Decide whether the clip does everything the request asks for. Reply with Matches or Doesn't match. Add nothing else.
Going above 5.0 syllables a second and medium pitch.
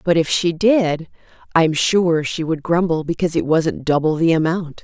Doesn't match